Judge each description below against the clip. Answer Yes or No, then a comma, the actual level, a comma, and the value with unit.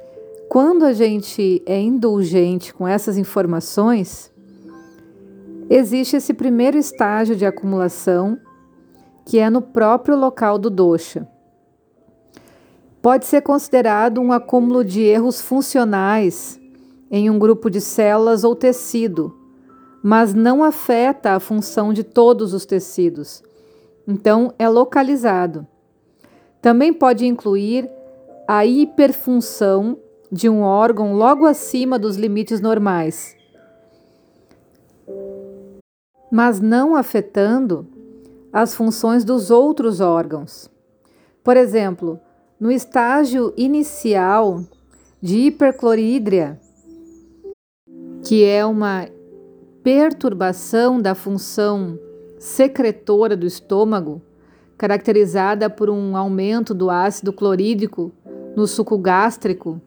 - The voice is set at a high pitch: Yes, high, 215 Hz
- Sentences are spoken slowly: Yes, slow, 95 wpm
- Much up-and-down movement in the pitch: No, average, 4.6 semitones